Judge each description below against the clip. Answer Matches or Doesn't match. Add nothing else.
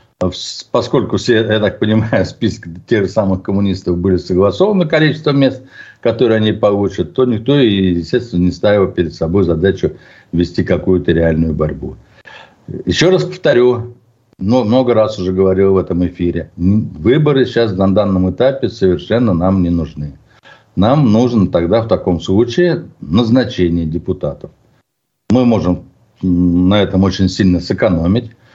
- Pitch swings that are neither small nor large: Matches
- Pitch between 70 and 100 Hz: Matches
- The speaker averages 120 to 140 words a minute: Matches